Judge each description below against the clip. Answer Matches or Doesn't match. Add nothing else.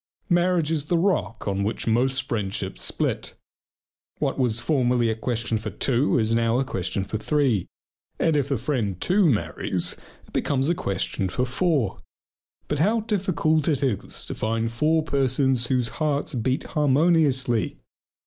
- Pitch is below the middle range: Matches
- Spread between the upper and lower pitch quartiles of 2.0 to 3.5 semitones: Doesn't match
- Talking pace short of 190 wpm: Matches